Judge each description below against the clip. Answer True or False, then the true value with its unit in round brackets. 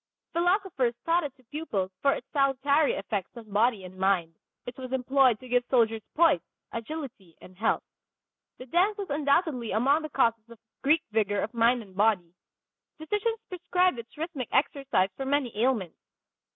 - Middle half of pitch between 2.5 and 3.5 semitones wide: False (5.6 semitones)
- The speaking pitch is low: False (255 Hz)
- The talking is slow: False (165 wpm)